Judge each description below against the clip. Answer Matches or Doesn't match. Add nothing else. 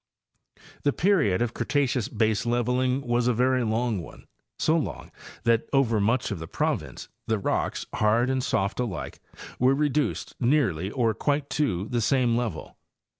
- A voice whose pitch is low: Matches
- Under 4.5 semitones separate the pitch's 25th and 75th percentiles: Matches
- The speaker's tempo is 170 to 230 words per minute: Doesn't match